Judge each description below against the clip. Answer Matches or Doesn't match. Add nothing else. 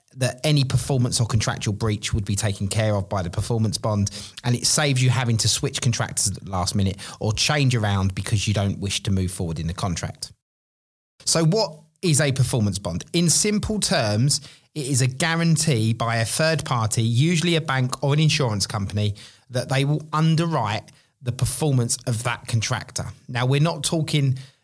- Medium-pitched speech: Doesn't match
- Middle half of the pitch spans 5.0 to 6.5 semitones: Matches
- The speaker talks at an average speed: Matches